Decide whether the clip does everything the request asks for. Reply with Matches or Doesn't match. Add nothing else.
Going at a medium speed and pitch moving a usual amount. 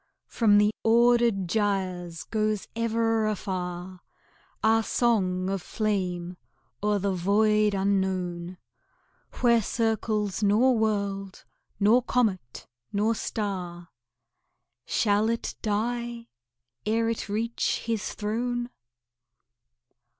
Doesn't match